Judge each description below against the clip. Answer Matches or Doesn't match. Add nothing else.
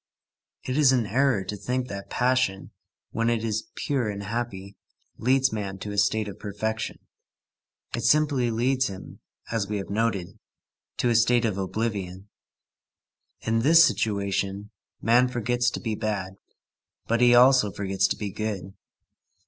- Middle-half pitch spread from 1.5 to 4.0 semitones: Matches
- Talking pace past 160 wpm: Doesn't match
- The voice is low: Matches